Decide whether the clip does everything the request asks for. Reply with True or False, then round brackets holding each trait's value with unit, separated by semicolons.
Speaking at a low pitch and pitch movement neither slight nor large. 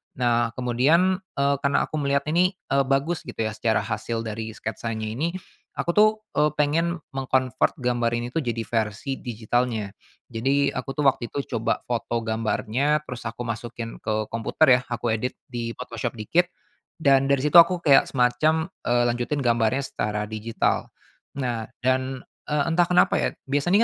True (125 Hz; 3.7 semitones)